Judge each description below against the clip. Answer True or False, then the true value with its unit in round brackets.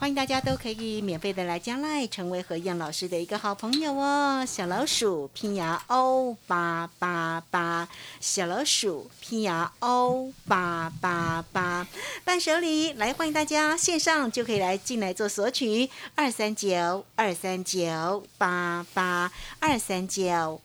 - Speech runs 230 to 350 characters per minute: False (215 characters per minute)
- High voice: True (200 Hz)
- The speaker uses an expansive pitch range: True (6.7 semitones)